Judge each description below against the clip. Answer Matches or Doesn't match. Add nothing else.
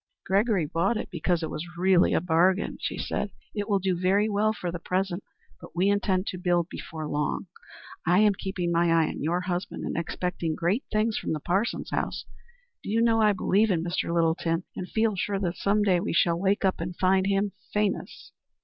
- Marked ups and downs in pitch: Doesn't match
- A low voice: Doesn't match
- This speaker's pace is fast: Matches